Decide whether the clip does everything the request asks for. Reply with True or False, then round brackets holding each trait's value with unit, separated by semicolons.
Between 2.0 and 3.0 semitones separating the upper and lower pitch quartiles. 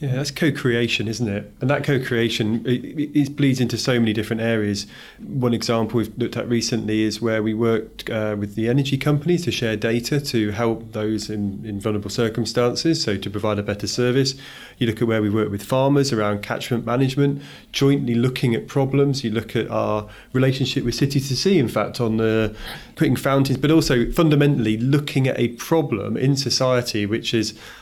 False (3.6 semitones)